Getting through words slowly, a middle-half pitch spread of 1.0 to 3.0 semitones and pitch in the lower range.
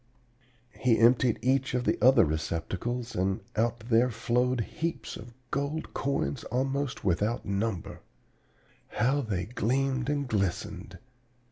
No: slow, 120 wpm; average, 3.5 semitones; low, 120 Hz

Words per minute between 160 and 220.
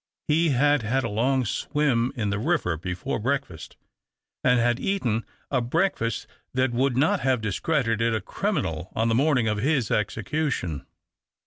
No: average, 150 wpm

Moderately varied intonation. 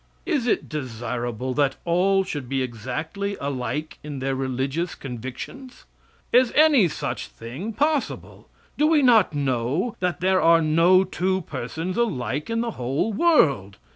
No: wide, 7.4 semitones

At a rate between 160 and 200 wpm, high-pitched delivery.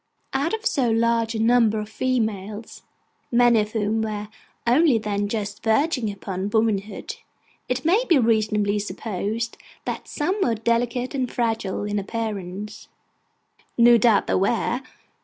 No: average, 140 wpm; high, 225 Hz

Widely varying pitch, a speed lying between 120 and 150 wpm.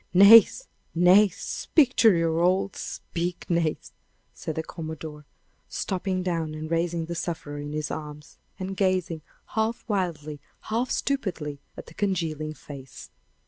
No: average, 3.6 semitones; slow, 135 wpm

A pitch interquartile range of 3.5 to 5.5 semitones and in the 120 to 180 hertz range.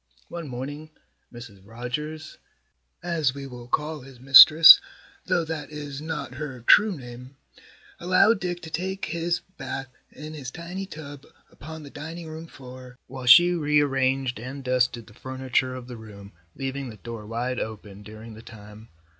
Yes: average, 4.2 semitones; low, 135 Hz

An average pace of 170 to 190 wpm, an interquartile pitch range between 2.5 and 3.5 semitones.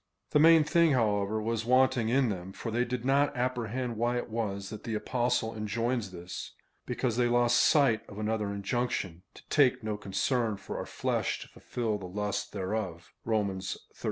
Yes: average, 185 wpm; average, 3.2 semitones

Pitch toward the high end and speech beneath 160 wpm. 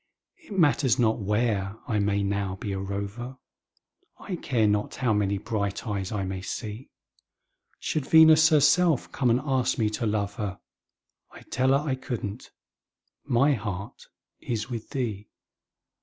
No: low, 110 Hz; average, 150 wpm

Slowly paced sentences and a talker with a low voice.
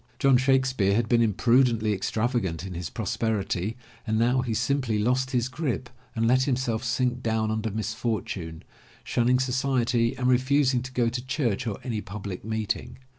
No: average, 160 wpm; low, 120 Hz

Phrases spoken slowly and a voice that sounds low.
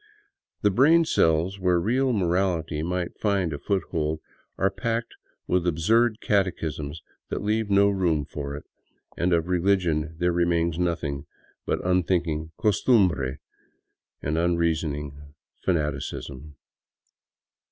Yes: slow, 120 wpm; very low, 85 Hz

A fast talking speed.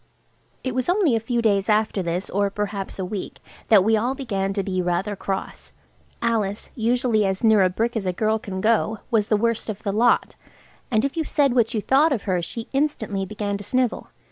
Yes: fast, 215 wpm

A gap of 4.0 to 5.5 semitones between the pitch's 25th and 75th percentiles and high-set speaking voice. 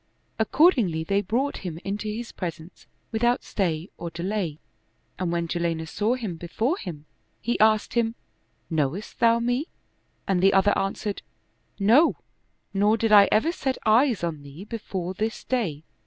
Yes: average, 5.0 semitones; high, 205 Hz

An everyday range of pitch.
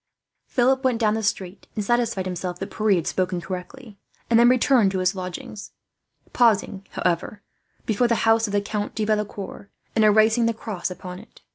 Yes: average, 3.4 semitones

